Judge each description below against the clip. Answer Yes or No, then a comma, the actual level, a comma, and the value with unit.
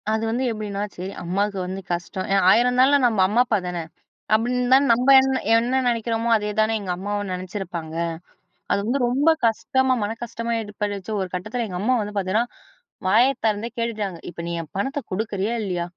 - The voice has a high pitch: Yes, high, 215 Hz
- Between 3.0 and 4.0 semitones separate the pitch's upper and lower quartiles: Yes, average, 3.7 semitones